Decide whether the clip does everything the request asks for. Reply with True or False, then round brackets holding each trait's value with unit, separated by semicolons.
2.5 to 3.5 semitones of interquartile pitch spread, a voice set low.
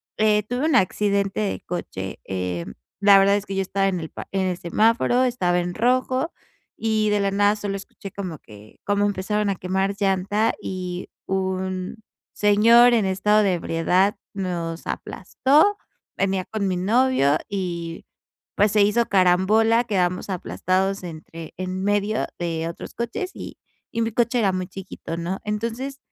False (2.8 semitones; 195 Hz)